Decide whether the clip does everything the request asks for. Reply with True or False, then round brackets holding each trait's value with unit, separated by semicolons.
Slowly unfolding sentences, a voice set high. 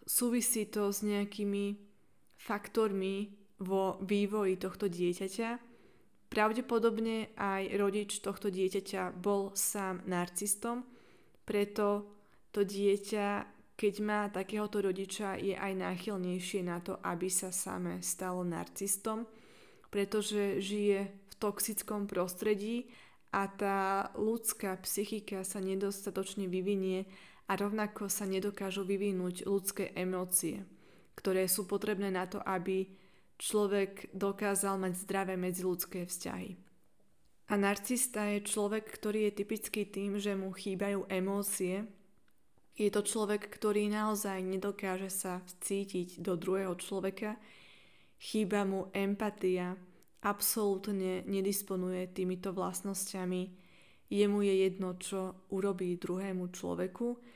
True (105 wpm; 200 Hz)